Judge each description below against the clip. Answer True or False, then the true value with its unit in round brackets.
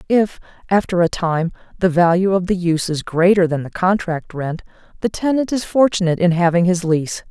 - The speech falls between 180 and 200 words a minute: True (190 wpm)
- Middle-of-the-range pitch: True (180 Hz)